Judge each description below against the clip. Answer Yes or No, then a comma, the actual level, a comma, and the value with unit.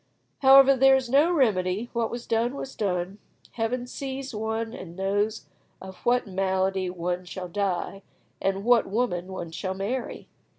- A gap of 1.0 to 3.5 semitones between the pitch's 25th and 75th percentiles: No, average, 4.8 semitones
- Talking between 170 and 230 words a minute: No, average, 155 wpm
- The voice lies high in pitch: Yes, high, 210 Hz